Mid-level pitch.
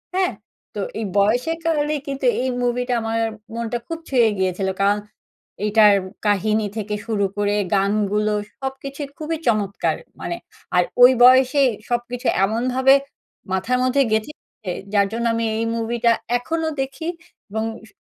No: high, 235 Hz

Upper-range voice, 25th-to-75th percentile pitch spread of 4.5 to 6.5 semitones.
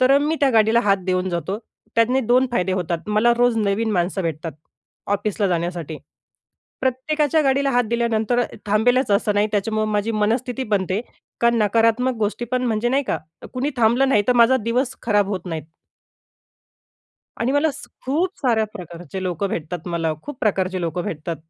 Yes: high, 220 Hz; average, 4.9 semitones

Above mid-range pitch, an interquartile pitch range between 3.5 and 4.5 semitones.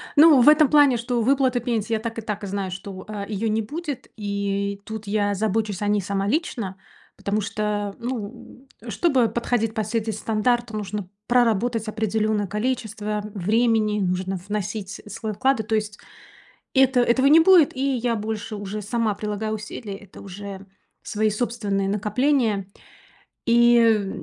No: high, 215 Hz; average, 2.8 semitones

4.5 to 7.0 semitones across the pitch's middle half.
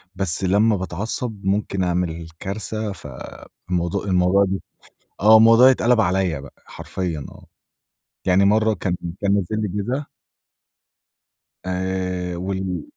No: average, 2.8 semitones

